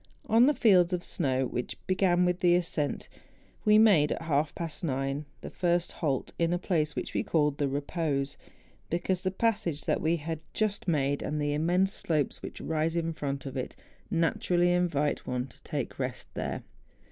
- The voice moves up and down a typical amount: Yes, average, 3.5 semitones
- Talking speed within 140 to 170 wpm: No, average, 180 wpm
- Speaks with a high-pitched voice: No, medium, 165 Hz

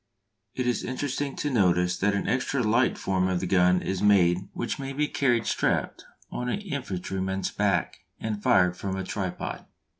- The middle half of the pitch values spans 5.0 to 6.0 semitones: Yes, wide, 5.5 semitones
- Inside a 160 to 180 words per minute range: Yes, average, 175 wpm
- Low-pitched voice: Yes, low, 100 Hz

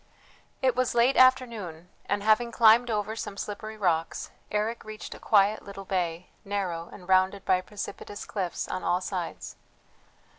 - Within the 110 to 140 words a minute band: No, average, 150 wpm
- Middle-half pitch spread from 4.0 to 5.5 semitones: No, average, 3.2 semitones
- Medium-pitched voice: No, high, 205 Hz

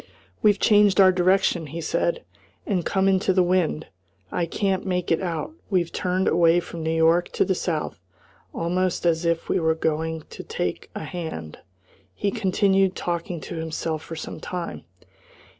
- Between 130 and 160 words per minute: No, average, 170 wpm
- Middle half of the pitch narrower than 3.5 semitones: Yes, narrow, 2.6 semitones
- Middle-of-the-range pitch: Yes, medium, 175 Hz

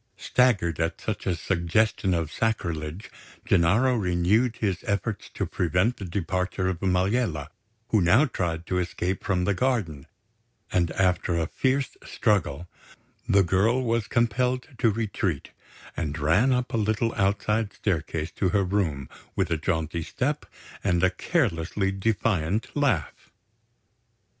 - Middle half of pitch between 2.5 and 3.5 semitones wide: No, average, 4.7 semitones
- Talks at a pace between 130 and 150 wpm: Yes, slow, 135 wpm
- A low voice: Yes, very low, 95 Hz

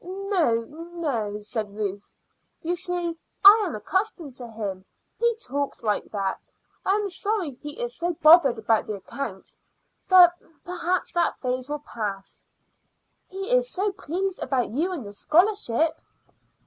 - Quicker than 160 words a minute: No, average, 145 wpm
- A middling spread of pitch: No, wide, 8.5 semitones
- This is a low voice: No, very high, 320 Hz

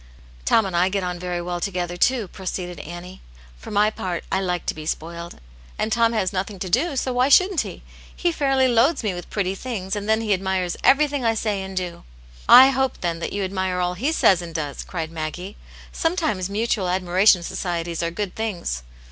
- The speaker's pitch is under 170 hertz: No, high, 190 Hz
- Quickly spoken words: Yes, fast, 220 wpm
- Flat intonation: No, average, 4.2 semitones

